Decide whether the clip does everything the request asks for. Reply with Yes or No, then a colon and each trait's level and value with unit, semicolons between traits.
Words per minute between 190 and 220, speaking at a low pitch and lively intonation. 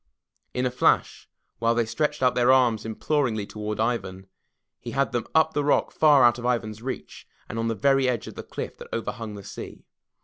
No: fast, 205 wpm; low, 120 Hz; average, 3.1 semitones